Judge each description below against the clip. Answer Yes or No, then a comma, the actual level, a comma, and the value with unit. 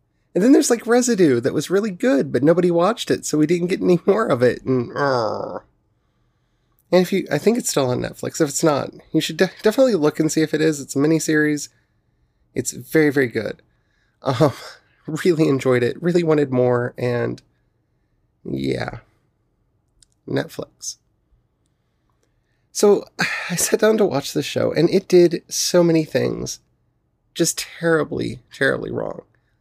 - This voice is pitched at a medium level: Yes, medium, 160 Hz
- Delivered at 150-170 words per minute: Yes, average, 160 wpm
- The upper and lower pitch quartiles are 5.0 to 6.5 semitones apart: Yes, average, 5.3 semitones